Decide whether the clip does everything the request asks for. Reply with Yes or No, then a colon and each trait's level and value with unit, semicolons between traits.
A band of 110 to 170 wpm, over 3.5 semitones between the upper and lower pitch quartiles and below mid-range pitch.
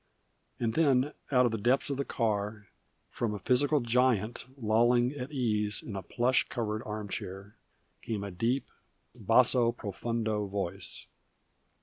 No: average, 140 wpm; average, 3.2 semitones; low, 115 Hz